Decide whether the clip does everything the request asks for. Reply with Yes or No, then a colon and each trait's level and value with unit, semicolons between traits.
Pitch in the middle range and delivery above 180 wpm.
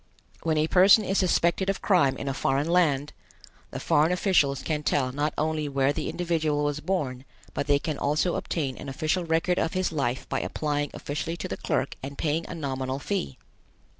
Yes: medium, 150 Hz; average, 195 wpm